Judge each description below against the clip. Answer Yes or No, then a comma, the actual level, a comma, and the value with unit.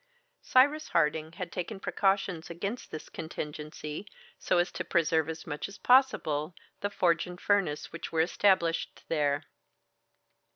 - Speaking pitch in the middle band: Yes, medium, 170 Hz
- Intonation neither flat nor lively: Yes, average, 3.9 semitones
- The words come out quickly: No, slow, 135 wpm